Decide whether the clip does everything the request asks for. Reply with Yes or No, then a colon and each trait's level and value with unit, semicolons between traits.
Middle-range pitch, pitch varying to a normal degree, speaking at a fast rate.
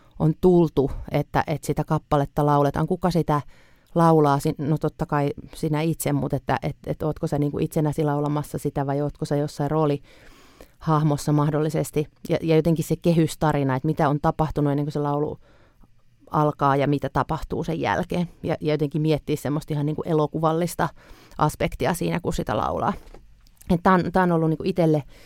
No: medium, 150 Hz; narrow, 1.6 semitones; fast, 160 wpm